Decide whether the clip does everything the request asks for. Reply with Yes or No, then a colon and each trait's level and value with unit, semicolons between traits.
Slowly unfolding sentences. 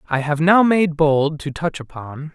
No: fast, 205 wpm